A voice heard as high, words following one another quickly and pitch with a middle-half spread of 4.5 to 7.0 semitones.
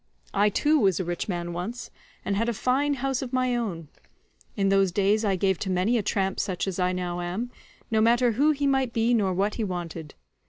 Yes: high, 205 Hz; fast, 225 wpm; average, 4.8 semitones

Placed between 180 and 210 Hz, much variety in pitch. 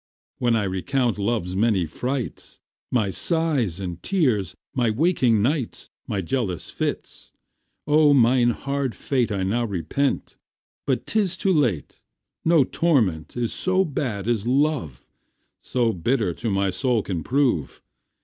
No: low, 120 Hz; wide, 6.0 semitones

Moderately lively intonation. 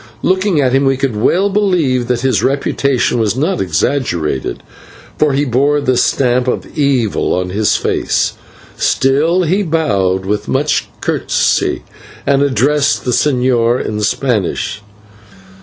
Yes: average, 4.6 semitones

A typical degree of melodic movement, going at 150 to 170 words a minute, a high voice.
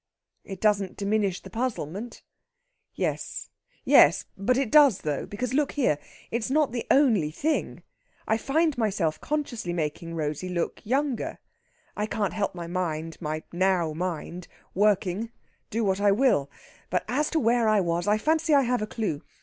No: wide, 6.1 semitones; average, 160 wpm; high, 205 Hz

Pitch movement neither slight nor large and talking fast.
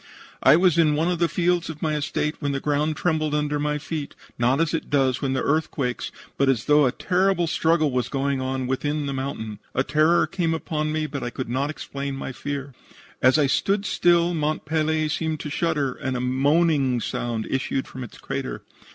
Yes: average, 3.0 semitones; fast, 210 wpm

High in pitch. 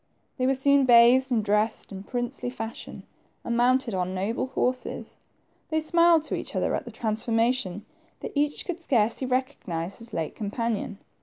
Yes: high, 240 Hz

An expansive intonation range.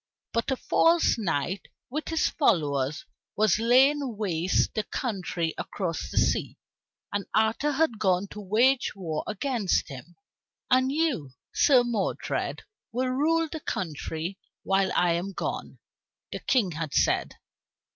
Yes: wide, 6.8 semitones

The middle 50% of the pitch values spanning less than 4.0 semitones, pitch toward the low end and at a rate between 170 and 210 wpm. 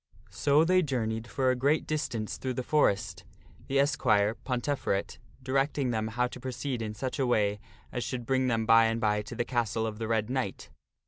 Yes: average, 3.1 semitones; low, 120 Hz; average, 195 wpm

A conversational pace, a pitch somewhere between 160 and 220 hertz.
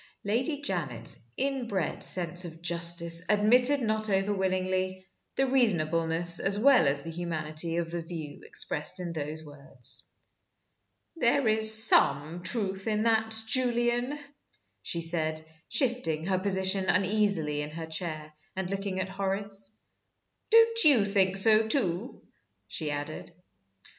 No: slow, 130 wpm; medium, 185 Hz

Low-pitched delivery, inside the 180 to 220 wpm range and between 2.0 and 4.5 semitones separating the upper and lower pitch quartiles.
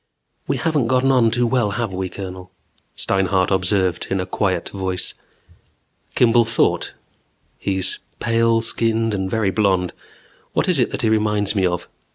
No: low, 105 Hz; average, 155 wpm; average, 3.5 semitones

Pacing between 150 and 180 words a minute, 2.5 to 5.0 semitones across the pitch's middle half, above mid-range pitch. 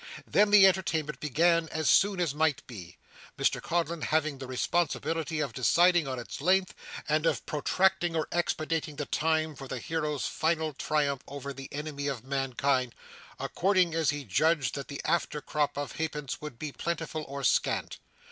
No: average, 170 wpm; average, 2.9 semitones; medium, 155 Hz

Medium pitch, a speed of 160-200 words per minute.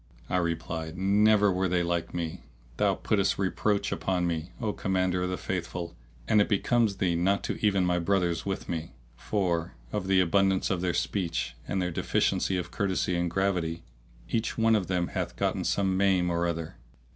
No: very low, 90 Hz; average, 180 wpm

